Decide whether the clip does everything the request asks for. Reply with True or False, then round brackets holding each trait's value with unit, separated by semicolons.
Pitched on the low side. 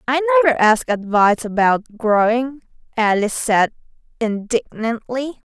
False (240 Hz)